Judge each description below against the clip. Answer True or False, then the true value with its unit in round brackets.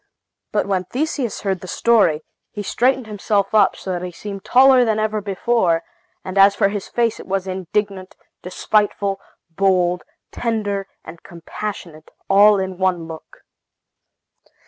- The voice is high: True (195 Hz)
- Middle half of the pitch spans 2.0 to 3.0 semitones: True (2.6 semitones)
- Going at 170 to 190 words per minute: False (145 wpm)